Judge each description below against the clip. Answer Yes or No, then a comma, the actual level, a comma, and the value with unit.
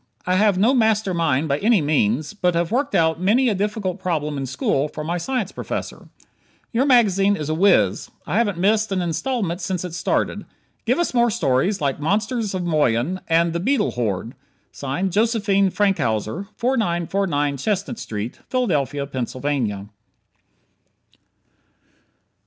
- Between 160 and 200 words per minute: No, average, 145 wpm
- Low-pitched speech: No, medium, 180 Hz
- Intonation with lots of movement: Yes, wide, 6.2 semitones